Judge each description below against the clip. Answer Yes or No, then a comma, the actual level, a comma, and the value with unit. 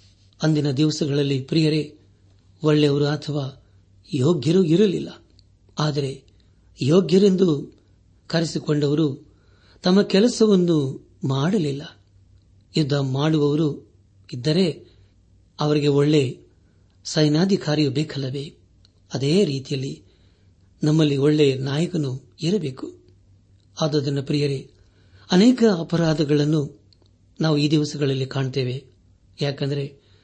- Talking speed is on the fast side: No, average, 70 wpm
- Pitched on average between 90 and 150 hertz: Yes, medium, 140 Hz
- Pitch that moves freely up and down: Yes, wide, 7.7 semitones